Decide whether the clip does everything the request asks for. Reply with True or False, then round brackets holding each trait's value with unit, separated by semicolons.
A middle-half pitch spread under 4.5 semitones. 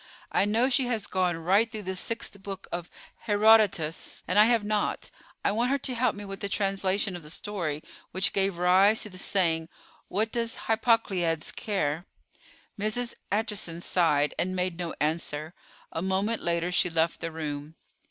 True (4.0 semitones)